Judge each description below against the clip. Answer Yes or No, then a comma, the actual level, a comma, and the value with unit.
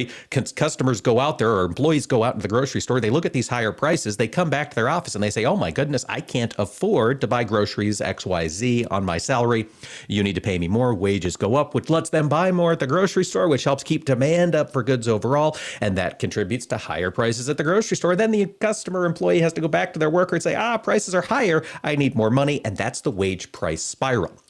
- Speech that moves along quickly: Yes, fast, 250 wpm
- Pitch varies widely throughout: Yes, wide, 6.9 semitones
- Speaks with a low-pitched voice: Yes, low, 130 Hz